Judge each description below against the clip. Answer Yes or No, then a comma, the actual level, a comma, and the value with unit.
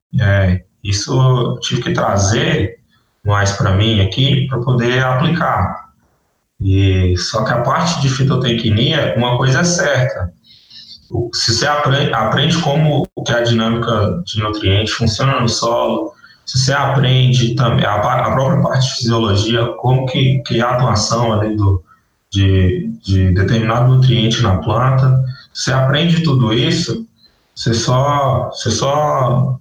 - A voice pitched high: No, low, 120 Hz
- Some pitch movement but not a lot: Yes, average, 3.7 semitones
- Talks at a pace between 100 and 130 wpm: No, average, 140 wpm